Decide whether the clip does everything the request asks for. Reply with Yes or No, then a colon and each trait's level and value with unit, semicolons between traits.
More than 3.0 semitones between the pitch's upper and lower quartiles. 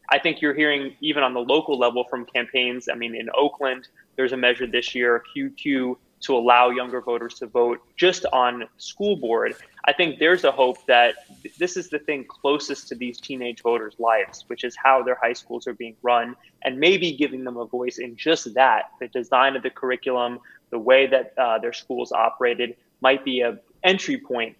No: narrow, 2.6 semitones